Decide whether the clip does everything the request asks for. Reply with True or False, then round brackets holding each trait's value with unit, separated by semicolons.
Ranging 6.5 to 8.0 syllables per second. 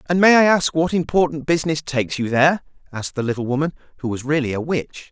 True (6.7 syllables/s)